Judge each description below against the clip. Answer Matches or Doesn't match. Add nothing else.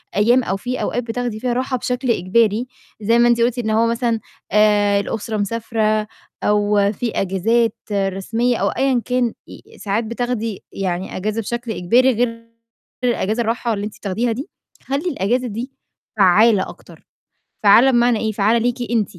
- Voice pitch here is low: Doesn't match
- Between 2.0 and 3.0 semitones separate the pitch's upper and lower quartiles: Matches